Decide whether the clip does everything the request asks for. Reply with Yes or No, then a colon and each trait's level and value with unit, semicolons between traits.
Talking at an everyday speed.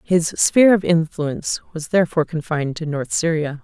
Yes: average, 165 wpm